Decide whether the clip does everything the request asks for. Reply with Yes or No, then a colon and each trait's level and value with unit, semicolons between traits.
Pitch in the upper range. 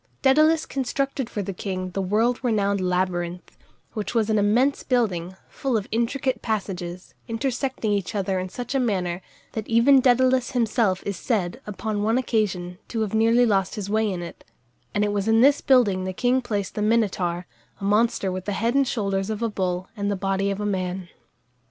Yes: high, 210 Hz